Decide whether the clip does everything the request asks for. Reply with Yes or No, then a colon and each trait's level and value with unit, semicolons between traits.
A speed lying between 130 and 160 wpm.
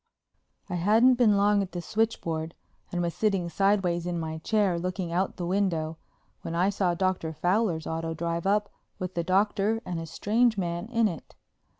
No: average, 185 wpm